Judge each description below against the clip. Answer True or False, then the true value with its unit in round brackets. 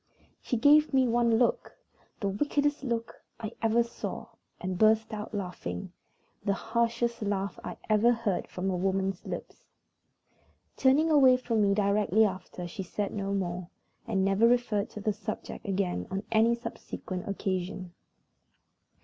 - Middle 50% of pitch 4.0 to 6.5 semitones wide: False (3.4 semitones)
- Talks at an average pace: True (145 wpm)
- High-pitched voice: True (210 Hz)